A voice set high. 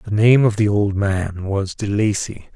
No: low, 105 Hz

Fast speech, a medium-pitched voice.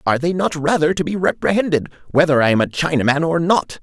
Yes: fast, 220 wpm; medium, 160 Hz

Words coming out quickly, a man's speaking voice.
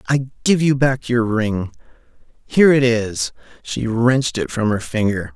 No: average, 155 wpm; male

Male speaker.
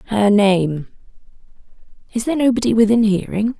No: female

